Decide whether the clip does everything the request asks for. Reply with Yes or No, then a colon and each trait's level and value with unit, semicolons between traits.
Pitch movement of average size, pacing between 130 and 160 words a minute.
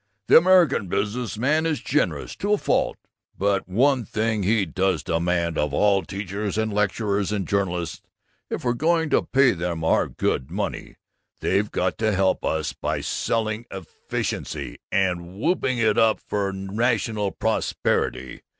Yes: average, 3.7 semitones; average, 150 wpm